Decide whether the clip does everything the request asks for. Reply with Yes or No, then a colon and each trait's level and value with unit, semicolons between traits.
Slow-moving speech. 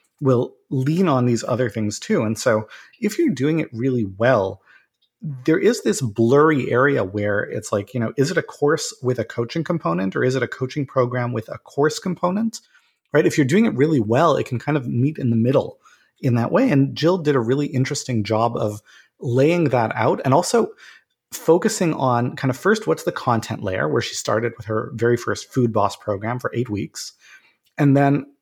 No: fast, 205 wpm